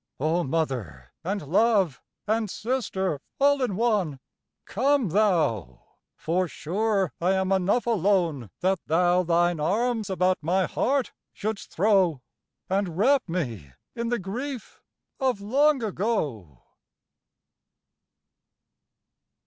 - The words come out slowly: Yes, slow, 110 wpm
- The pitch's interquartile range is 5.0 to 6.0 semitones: Yes, average, 5.3 semitones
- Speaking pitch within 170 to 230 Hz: Yes, high, 190 Hz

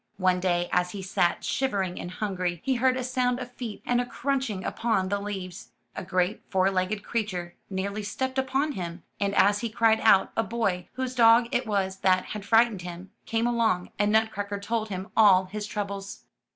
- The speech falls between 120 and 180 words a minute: No, average, 195 wpm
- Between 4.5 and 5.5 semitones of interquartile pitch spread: No, average, 3.7 semitones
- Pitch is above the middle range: Yes, high, 205 Hz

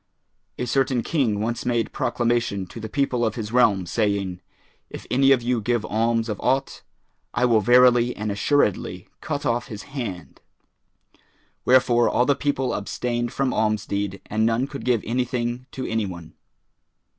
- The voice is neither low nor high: No, low, 120 Hz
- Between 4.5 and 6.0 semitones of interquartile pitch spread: No, average, 2.9 semitones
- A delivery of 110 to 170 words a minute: Yes, average, 160 wpm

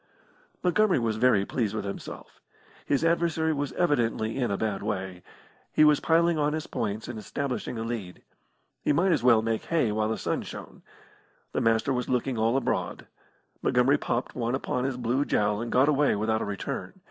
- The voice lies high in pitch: No, low, 120 Hz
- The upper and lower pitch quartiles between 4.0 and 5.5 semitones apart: Yes, average, 4.7 semitones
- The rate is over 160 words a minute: Yes, average, 185 wpm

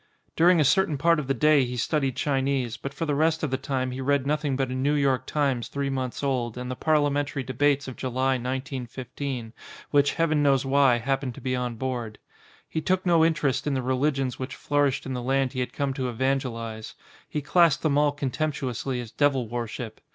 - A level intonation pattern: Yes, narrow, 2.3 semitones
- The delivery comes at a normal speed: No, fast, 210 wpm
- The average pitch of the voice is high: No, low, 135 Hz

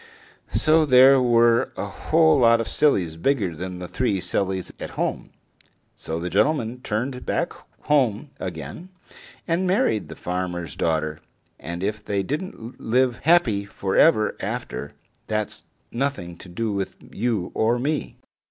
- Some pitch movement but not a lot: No, wide, 6.7 semitones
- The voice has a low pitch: Yes, low, 110 Hz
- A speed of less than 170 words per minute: Yes, average, 145 wpm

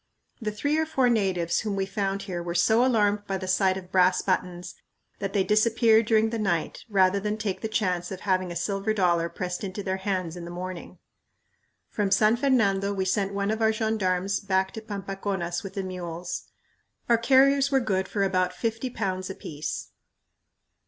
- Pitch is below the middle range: No, high, 195 Hz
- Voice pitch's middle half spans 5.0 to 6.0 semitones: No, average, 2.9 semitones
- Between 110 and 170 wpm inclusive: No, average, 185 wpm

